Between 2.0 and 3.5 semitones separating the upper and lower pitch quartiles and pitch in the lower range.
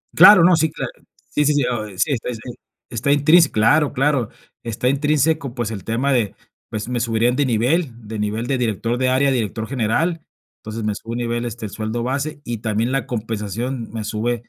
No: average, 4.0 semitones; low, 120 Hz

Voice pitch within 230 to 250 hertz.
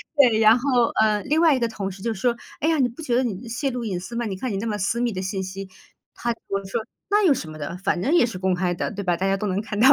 No: high, 220 Hz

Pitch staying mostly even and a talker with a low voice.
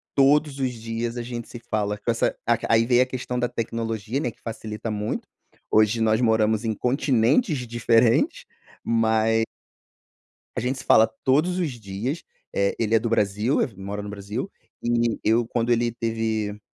Yes: narrow, 2.0 semitones; low, 115 Hz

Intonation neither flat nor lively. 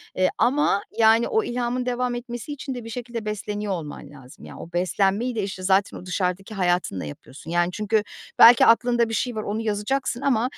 Yes: average, 4.5 semitones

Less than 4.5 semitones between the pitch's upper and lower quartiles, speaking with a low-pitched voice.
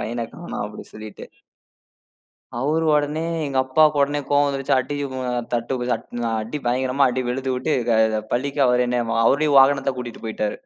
Yes: average, 2.8 semitones; low, 130 Hz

